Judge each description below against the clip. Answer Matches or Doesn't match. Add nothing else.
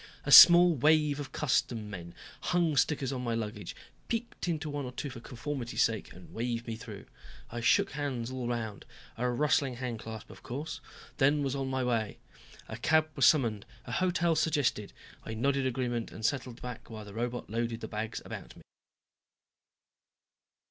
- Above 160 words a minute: Matches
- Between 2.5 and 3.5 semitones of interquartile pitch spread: Doesn't match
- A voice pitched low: Matches